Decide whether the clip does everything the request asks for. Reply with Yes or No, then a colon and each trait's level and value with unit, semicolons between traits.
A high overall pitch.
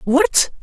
Yes: high, 245 Hz